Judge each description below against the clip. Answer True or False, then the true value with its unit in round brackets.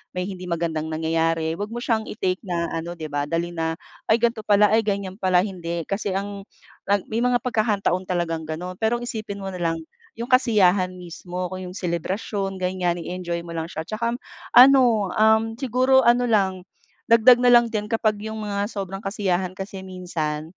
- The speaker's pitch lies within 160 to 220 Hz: True (190 Hz)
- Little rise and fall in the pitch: False (4.1 semitones)